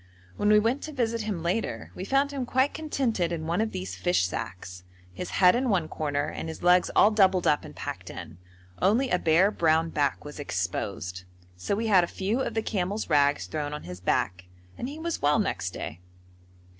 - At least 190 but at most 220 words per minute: Yes, fast, 205 wpm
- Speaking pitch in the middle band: Yes, medium, 180 Hz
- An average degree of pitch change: No, wide, 7.5 semitones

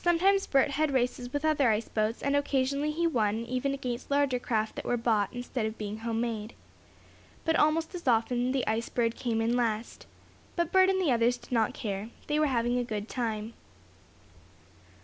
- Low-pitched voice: No, high, 245 Hz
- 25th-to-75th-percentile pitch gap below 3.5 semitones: No, average, 4.1 semitones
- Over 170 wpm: Yes, average, 190 wpm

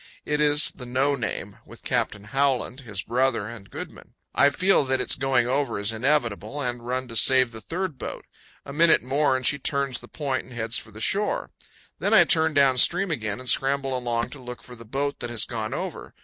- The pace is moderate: No, fast, 215 wpm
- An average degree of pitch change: Yes, average, 3.2 semitones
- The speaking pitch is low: Yes, low, 130 Hz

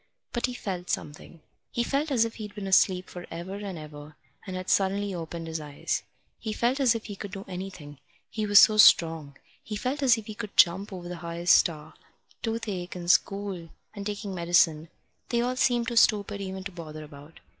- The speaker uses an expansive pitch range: No, average, 4.2 semitones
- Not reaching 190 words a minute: No, average, 200 wpm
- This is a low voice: No, high, 190 Hz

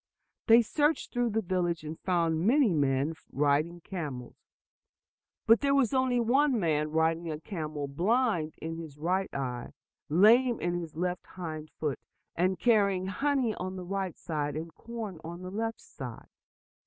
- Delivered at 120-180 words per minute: Yes, average, 155 wpm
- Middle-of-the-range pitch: Yes, medium, 180 Hz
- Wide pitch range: Yes, wide, 6.2 semitones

